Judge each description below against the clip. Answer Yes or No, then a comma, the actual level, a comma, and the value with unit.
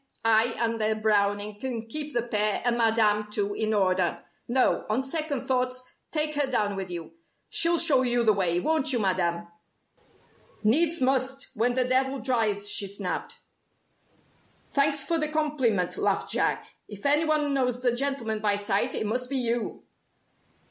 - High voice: Yes, high, 240 Hz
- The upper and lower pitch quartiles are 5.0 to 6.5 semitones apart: No, average, 4.4 semitones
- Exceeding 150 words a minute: Yes, average, 160 wpm